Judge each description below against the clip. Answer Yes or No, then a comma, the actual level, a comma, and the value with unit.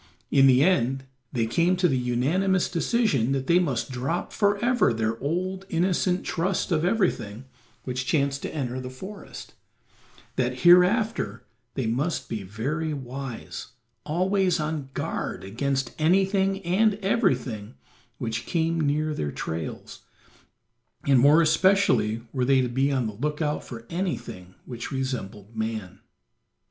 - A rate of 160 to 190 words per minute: No, slow, 135 wpm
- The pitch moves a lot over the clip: Yes, wide, 6.6 semitones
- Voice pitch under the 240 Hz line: Yes, medium, 140 Hz